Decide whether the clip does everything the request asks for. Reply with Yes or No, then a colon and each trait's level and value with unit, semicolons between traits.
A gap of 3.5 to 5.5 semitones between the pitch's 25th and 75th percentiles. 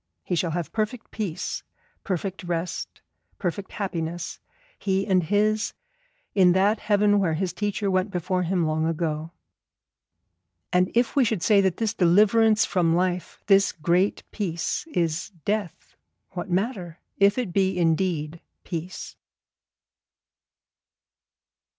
No: average, 3.1 semitones